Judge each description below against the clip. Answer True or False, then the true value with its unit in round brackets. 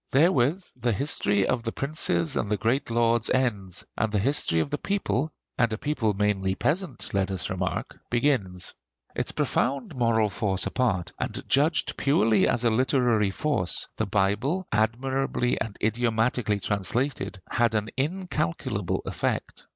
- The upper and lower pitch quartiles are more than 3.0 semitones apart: True (4.7 semitones)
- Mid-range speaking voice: False (115 Hz)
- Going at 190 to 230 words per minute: False (145 wpm)